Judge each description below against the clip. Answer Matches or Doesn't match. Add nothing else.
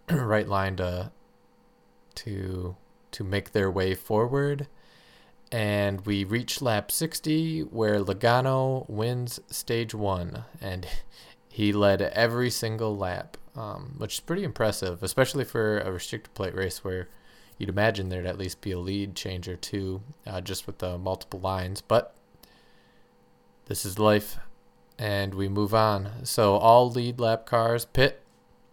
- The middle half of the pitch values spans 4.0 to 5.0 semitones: Doesn't match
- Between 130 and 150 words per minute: Matches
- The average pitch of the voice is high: Doesn't match